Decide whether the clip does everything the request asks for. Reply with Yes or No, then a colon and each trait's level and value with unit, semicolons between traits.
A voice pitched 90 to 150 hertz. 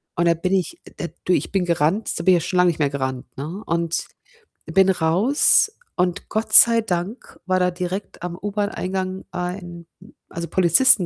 No: medium, 180 Hz